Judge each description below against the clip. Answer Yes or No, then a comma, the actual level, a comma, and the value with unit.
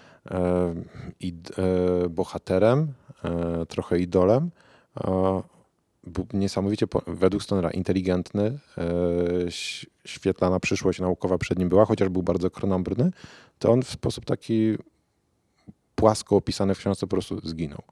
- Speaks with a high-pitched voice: No, very low, 95 Hz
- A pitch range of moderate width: Yes, average, 3.2 semitones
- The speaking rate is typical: No, slow, 100 wpm